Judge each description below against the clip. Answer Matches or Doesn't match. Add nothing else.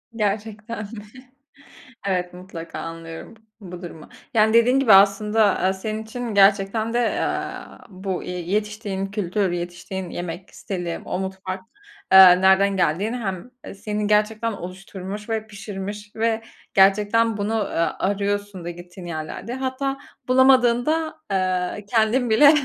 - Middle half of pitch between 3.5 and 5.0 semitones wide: Doesn't match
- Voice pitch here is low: Doesn't match